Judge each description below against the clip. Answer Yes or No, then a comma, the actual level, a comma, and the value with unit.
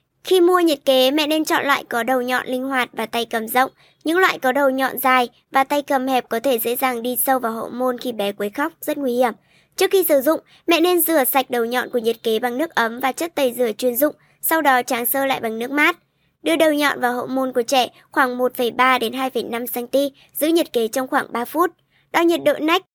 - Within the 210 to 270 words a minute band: Yes, average, 245 wpm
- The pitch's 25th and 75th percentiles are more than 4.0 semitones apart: No, average, 3.5 semitones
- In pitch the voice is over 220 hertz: Yes, very high, 260 Hz